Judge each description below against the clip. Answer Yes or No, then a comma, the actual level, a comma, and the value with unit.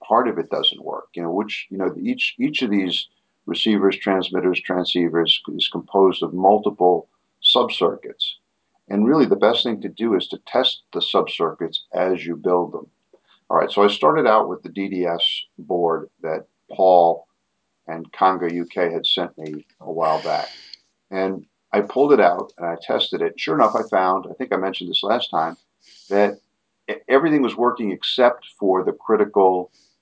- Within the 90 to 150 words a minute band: No, average, 175 wpm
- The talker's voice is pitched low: Yes, very low, 95 Hz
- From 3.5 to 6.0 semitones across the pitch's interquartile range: No, average, 2.8 semitones